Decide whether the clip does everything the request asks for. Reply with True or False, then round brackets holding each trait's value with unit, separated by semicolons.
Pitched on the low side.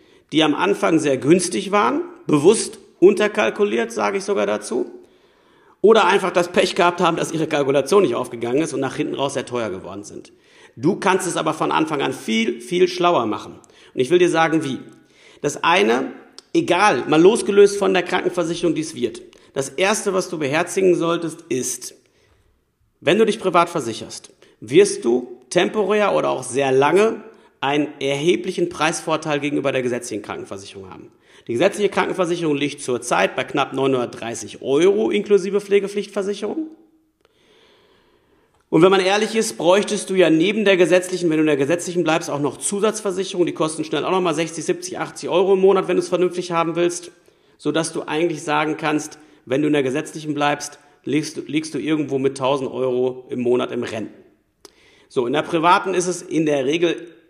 False (175 Hz)